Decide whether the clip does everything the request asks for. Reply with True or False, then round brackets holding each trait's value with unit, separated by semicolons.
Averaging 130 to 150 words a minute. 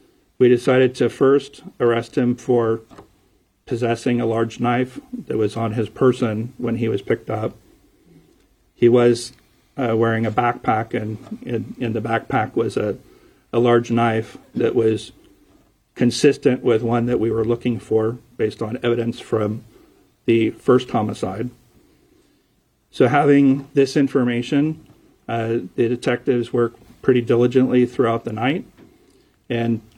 True (135 wpm)